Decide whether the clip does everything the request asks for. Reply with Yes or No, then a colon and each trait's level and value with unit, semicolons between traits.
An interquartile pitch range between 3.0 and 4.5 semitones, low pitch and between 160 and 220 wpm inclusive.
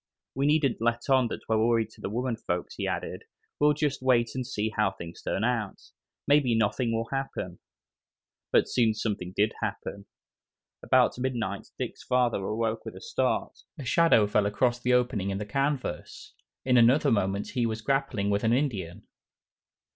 Yes: average, 3.7 semitones; low, 115 Hz; average, 165 wpm